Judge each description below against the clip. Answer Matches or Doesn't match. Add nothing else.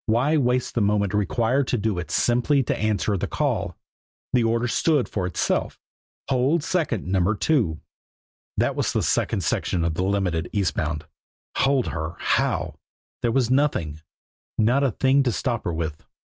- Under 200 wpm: Matches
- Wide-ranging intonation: Matches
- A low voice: Matches